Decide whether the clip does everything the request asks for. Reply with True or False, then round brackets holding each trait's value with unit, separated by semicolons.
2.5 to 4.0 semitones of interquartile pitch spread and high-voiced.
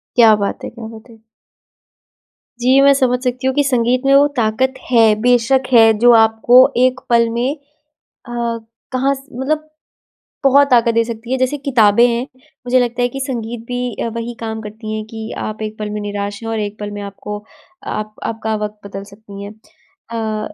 True (2.8 semitones; 230 Hz)